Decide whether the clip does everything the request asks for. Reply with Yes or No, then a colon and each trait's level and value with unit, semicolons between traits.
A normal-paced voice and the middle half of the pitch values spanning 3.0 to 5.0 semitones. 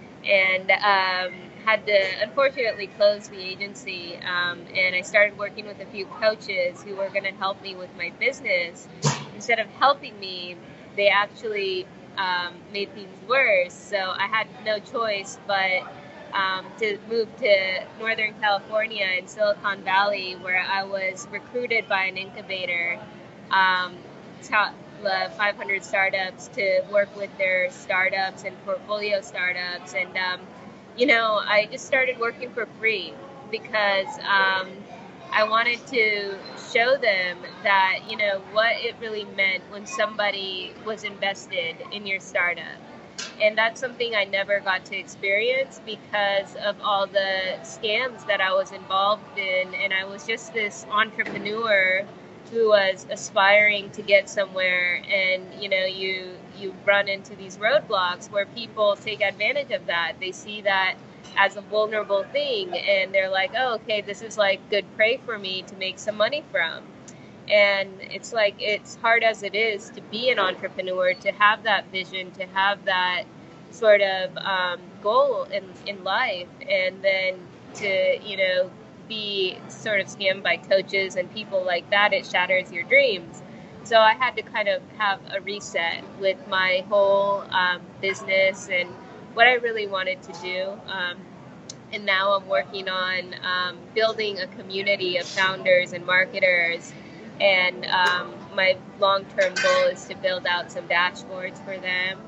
No: average, 155 wpm; narrow, 2.5 semitones